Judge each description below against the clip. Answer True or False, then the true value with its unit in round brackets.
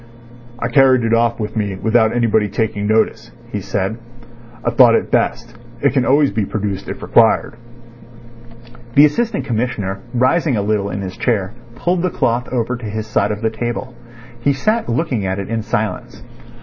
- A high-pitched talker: False (115 Hz)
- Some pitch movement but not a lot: True (3.1 semitones)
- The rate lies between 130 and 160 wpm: False (175 wpm)